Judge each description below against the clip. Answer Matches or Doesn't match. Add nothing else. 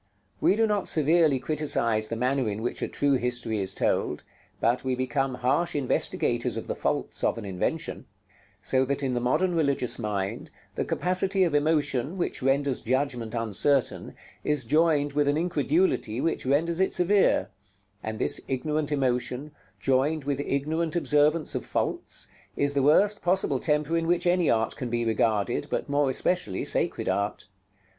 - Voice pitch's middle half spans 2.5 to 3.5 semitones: Doesn't match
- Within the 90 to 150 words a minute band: Doesn't match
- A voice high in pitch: Doesn't match